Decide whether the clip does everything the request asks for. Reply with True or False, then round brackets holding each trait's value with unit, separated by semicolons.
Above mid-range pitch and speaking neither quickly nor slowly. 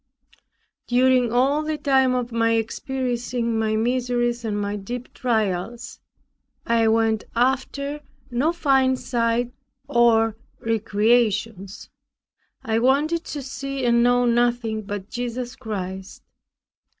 False (240 Hz; 110 wpm)